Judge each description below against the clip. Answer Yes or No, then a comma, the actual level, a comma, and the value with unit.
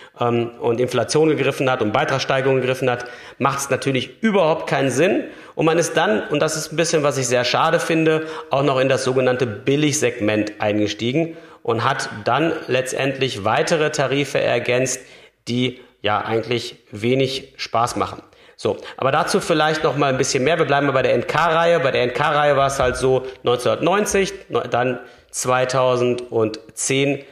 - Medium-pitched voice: No, low, 130 Hz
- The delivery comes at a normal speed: Yes, average, 160 wpm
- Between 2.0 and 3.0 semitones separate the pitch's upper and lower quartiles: No, average, 3.6 semitones